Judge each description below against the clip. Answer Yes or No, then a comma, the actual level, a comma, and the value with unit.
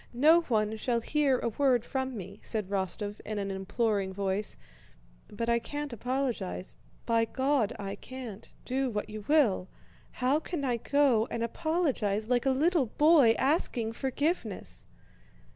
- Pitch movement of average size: Yes, average, 4.6 semitones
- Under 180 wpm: Yes, average, 145 wpm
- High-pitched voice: Yes, high, 235 Hz